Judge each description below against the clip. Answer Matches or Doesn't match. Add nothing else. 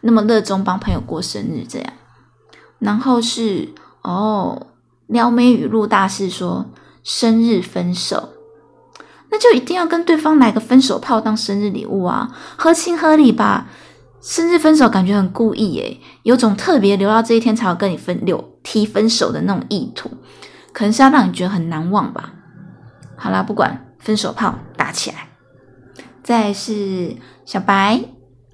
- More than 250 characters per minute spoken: Doesn't match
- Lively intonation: Doesn't match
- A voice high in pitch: Matches